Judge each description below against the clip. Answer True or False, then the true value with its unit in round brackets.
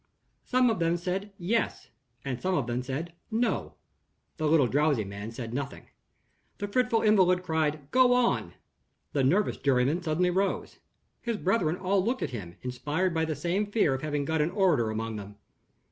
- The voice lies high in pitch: False (165 Hz)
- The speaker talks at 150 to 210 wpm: True (175 wpm)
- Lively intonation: True (6.5 semitones)